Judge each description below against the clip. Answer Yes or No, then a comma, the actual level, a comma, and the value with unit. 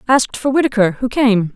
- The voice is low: No, high, 235 Hz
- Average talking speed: Yes, average, 195 wpm